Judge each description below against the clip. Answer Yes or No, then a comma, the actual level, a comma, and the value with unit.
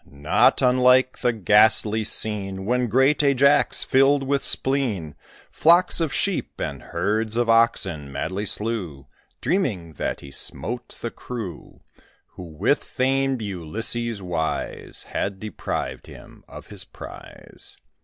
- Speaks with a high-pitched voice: No, low, 115 Hz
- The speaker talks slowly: Yes, slow, 125 wpm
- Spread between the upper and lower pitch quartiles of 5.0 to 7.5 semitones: Yes, wide, 5.4 semitones